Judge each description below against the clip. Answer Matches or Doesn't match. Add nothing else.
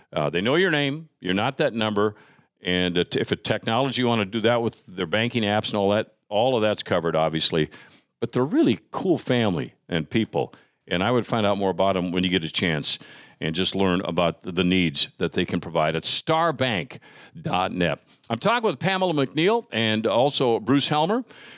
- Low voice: Matches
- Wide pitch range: Matches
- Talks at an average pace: Matches